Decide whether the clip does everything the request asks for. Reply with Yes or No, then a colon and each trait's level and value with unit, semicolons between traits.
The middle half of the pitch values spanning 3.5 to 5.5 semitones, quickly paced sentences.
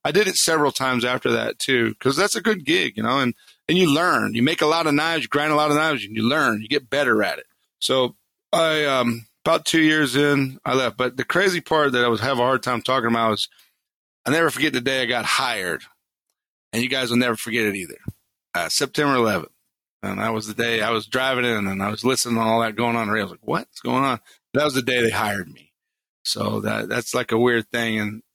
Yes: average, 4.2 semitones; fast, 260 wpm